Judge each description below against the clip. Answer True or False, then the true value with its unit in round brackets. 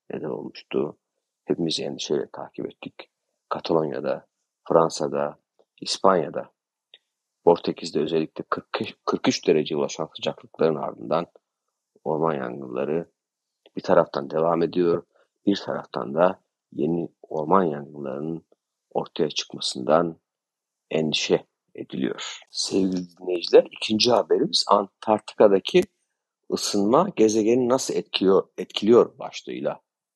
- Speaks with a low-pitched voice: True (85 Hz)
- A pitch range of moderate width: True (5.0 semitones)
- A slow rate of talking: True (85 wpm)